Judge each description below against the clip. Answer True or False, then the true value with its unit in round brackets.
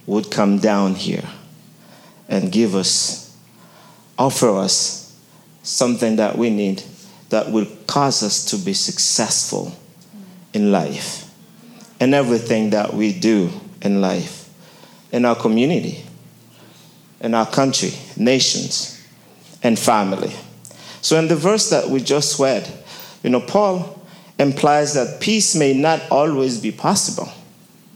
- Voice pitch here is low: False (145 Hz)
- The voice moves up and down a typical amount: False (8.6 semitones)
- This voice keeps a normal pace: False (120 wpm)